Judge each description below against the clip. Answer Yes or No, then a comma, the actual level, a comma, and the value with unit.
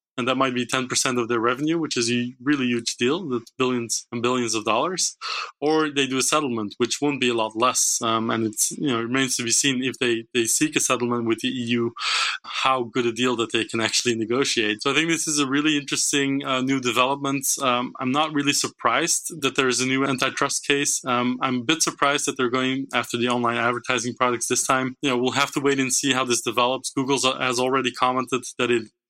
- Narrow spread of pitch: Yes, narrow, 2.3 semitones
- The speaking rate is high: Yes, fast, 235 wpm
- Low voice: Yes, low, 130 Hz